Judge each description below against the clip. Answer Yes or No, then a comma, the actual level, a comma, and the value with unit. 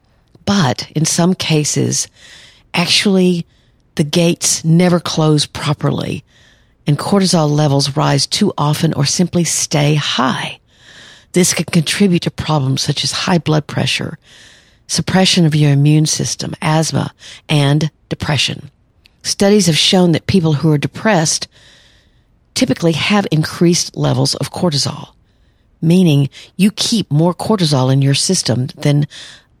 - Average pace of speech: No, slow, 125 wpm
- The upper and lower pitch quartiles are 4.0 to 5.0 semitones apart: No, average, 3.4 semitones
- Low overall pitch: No, medium, 155 Hz